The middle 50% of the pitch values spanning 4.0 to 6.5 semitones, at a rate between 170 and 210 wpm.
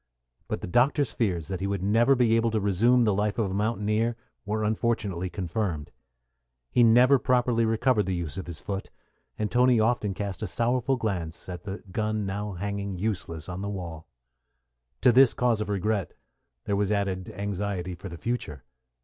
No: average, 3.5 semitones; average, 180 wpm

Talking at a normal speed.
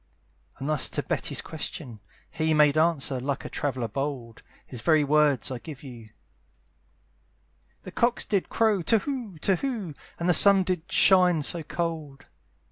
Yes: average, 160 wpm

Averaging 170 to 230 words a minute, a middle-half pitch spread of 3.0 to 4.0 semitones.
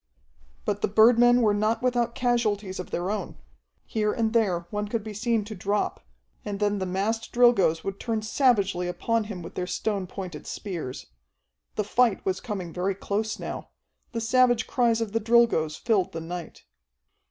Yes: average, 175 wpm; average, 3.4 semitones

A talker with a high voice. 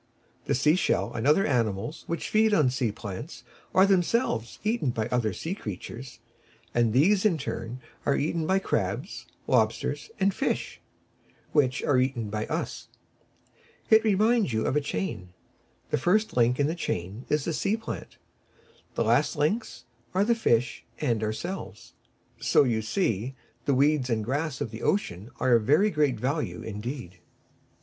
No: low, 135 Hz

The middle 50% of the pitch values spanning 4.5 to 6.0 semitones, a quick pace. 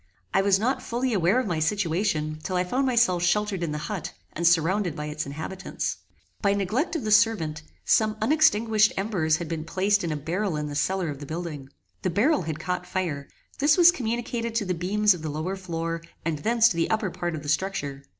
Yes: average, 5.1 semitones; fast, 215 wpm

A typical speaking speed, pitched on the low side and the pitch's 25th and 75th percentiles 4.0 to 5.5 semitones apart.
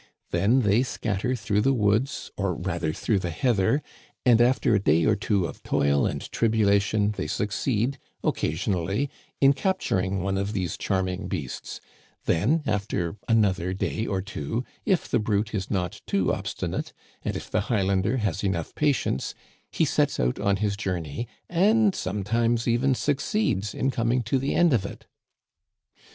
Yes: average, 160 wpm; low, 105 Hz; average, 4.3 semitones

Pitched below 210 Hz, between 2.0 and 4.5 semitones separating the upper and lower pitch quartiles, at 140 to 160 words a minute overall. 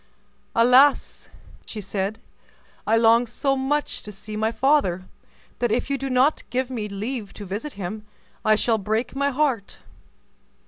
No: high, 230 Hz; average, 4.1 semitones; average, 150 wpm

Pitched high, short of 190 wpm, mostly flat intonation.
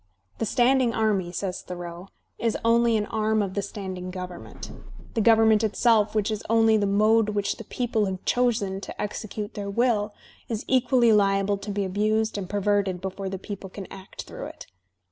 Yes: high, 210 Hz; average, 180 wpm; narrow, 2.3 semitones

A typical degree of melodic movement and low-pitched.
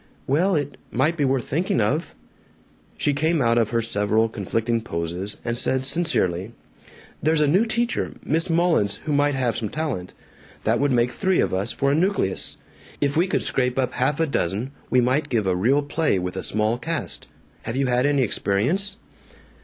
No: wide, 5.7 semitones; low, 130 Hz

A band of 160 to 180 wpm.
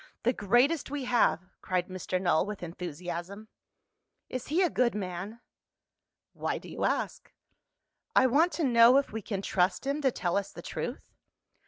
Yes: average, 165 wpm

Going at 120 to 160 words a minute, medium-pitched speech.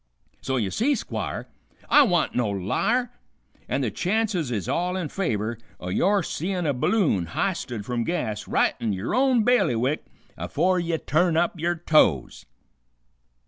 Yes: average, 150 wpm; medium, 165 Hz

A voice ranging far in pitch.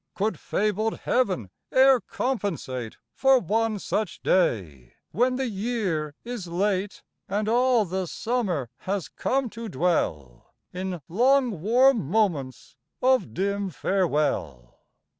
Yes: wide, 6.6 semitones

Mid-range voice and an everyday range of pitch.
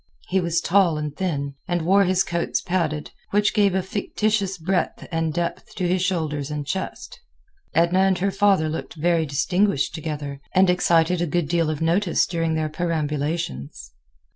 Yes: medium, 170 Hz; average, 3.3 semitones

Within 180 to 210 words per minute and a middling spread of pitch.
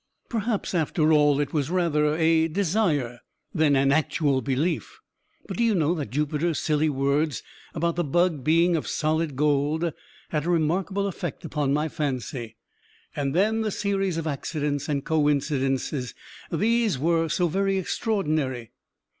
No: average, 145 wpm; average, 3.3 semitones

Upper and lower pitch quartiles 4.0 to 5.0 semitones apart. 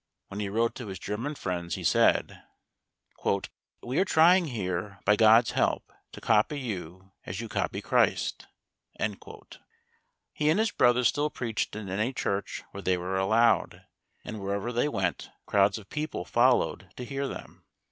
Yes: average, 4.6 semitones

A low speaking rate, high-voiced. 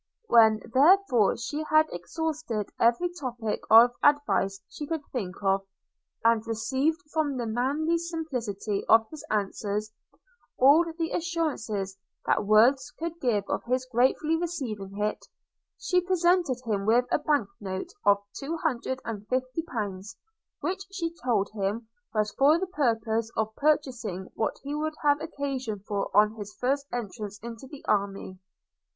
No: average, 145 wpm; high, 245 Hz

